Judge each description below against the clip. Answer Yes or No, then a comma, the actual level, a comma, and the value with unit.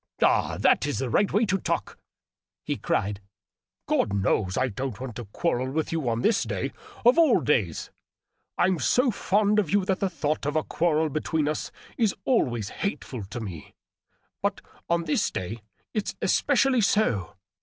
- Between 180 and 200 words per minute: Yes, average, 185 wpm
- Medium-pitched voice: Yes, medium, 155 Hz